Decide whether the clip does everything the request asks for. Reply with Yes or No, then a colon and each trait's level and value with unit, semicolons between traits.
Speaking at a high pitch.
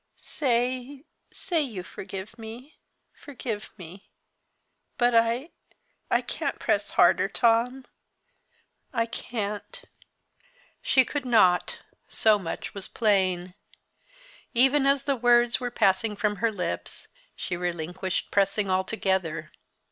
Yes: high, 225 Hz